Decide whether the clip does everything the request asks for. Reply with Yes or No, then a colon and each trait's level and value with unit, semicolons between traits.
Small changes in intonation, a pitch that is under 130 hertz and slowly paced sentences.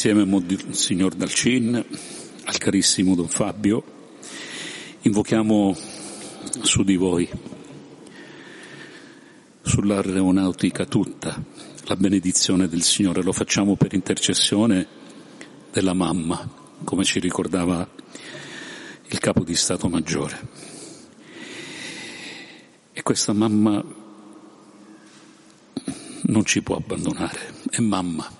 Yes: narrow, 2.2 semitones; very low, 95 Hz; slow, 85 wpm